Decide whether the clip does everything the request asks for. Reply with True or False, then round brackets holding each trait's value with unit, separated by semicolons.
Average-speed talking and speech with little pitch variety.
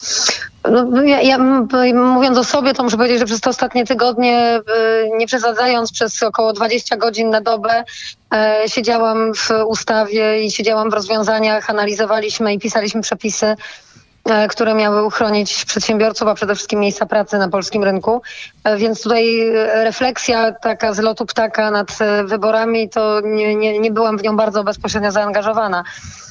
True (145 wpm; 1.3 semitones)